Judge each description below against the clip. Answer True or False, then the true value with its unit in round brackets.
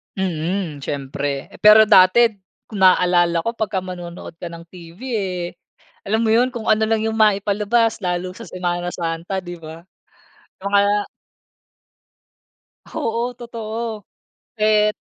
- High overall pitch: True (195 Hz)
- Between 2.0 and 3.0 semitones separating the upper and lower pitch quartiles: False (3.8 semitones)